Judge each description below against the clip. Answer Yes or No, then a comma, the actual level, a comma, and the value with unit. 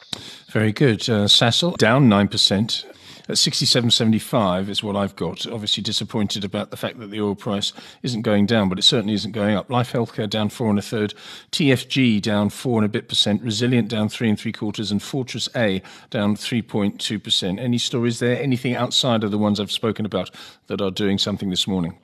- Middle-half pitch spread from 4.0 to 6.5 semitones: No, average, 2.7 semitones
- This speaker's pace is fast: Yes, fast, 210 wpm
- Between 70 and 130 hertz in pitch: Yes, low, 110 Hz